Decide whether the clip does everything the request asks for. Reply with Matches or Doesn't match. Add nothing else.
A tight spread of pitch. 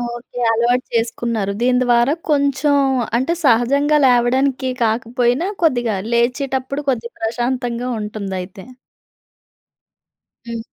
Matches